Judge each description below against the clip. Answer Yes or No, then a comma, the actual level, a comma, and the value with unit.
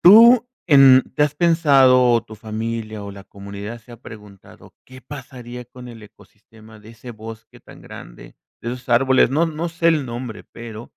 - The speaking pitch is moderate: No, low, 120 Hz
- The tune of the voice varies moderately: Yes, average, 3.8 semitones